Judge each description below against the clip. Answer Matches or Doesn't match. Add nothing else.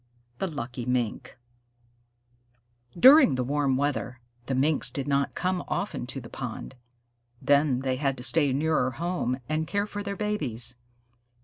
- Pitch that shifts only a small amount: Doesn't match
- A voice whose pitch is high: Doesn't match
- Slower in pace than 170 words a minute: Matches